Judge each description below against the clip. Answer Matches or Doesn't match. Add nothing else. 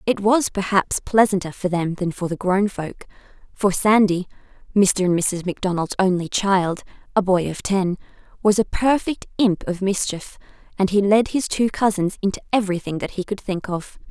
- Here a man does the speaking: Doesn't match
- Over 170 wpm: Matches